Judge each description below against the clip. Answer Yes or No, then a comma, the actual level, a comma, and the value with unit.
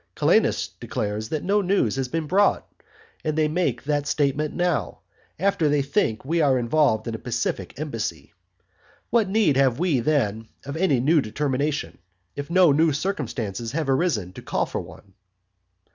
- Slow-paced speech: No, average, 165 wpm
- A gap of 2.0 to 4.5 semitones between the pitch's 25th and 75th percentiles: No, average, 5.3 semitones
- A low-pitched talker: No, medium, 145 Hz